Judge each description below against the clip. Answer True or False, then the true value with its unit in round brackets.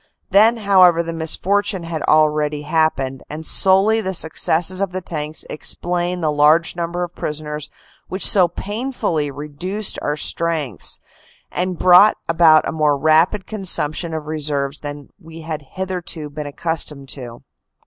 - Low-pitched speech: False (165 Hz)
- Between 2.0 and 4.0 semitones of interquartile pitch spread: True (3.4 semitones)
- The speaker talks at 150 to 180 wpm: False (140 wpm)